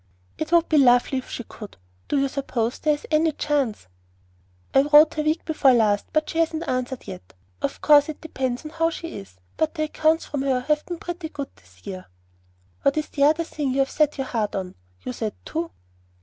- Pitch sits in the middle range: No, very high, 290 Hz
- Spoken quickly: Yes, fast, 215 wpm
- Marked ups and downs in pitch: No, average, 4.0 semitones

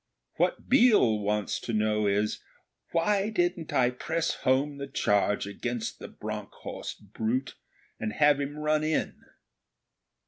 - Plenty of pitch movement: Yes, wide, 6.8 semitones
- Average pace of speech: No, slow, 130 wpm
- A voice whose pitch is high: No, low, 135 Hz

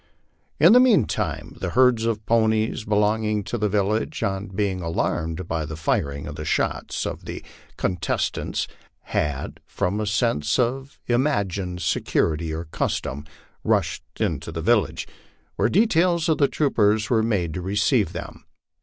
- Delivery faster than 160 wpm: No, average, 145 wpm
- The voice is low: Yes, low, 105 Hz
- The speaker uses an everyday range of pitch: No, wide, 5.9 semitones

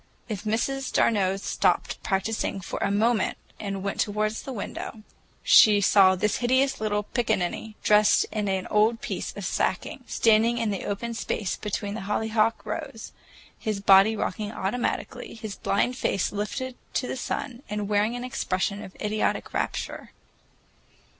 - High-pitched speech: Yes, high, 215 Hz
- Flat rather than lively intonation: Yes, narrow, 2.2 semitones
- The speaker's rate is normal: Yes, average, 150 wpm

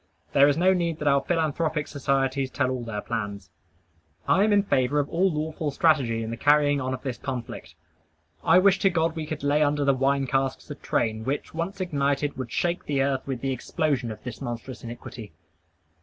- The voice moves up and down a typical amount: Yes, average, 3.4 semitones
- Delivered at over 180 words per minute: Yes, average, 200 wpm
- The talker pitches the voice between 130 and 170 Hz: Yes, medium, 140 Hz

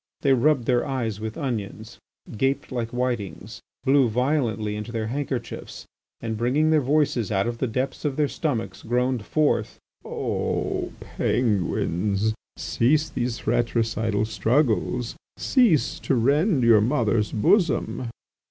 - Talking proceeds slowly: Yes, slow, 125 wpm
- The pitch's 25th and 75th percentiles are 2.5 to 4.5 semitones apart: Yes, average, 3.9 semitones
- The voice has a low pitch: Yes, low, 120 Hz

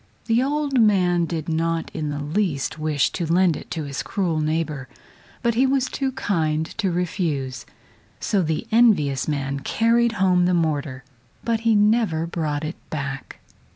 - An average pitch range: No, wide, 5.8 semitones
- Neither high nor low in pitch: Yes, medium, 165 Hz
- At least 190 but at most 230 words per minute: No, average, 160 wpm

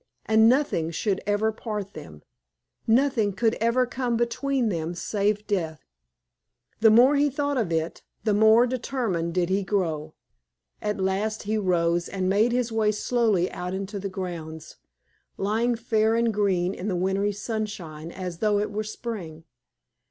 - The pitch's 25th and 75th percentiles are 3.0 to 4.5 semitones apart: Yes, average, 3.9 semitones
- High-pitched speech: Yes, high, 210 Hz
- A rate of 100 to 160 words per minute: Yes, average, 155 wpm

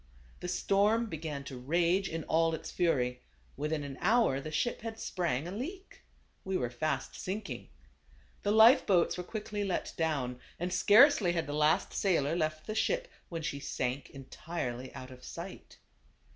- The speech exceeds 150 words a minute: Yes, average, 160 wpm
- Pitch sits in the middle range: Yes, medium, 165 Hz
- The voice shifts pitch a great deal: Yes, wide, 6.0 semitones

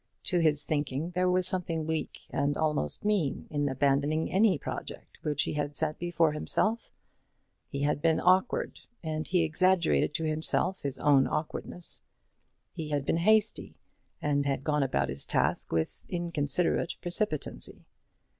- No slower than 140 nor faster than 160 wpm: Yes, average, 145 wpm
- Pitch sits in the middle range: Yes, medium, 155 Hz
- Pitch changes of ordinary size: Yes, average, 3.3 semitones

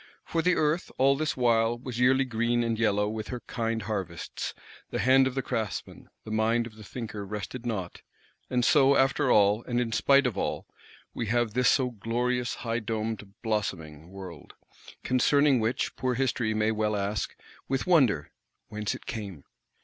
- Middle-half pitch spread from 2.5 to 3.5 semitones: Yes, average, 3.1 semitones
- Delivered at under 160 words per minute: No, average, 170 wpm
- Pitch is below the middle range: Yes, low, 115 Hz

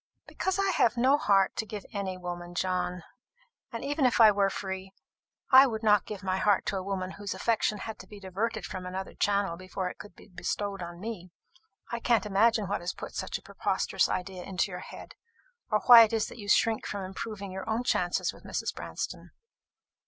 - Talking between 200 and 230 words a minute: Yes, fast, 205 wpm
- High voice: Yes, high, 200 Hz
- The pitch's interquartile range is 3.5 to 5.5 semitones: No, average, 3.0 semitones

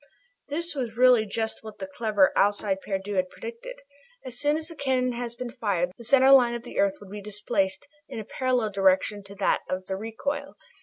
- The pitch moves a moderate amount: Yes, average, 4.7 semitones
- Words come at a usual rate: No, fast, 210 wpm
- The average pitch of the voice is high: Yes, high, 225 Hz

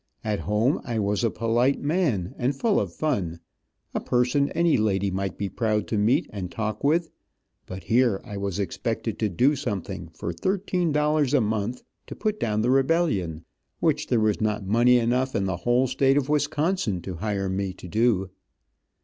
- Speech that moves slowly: No, average, 185 wpm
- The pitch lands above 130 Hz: No, low, 115 Hz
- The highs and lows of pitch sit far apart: Yes, wide, 5.9 semitones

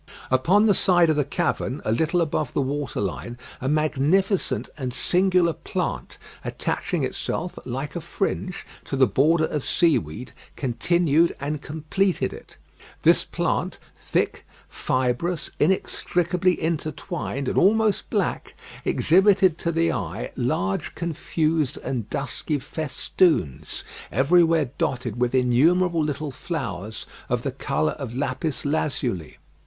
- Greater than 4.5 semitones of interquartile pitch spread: Yes, average, 5.0 semitones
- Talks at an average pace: No, slow, 125 wpm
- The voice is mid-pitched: Yes, medium, 150 Hz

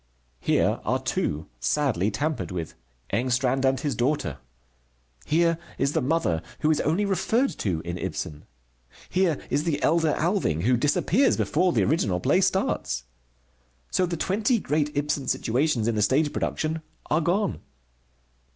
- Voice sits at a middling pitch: Yes, medium, 145 Hz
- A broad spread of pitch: Yes, wide, 7.2 semitones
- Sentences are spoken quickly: No, average, 145 wpm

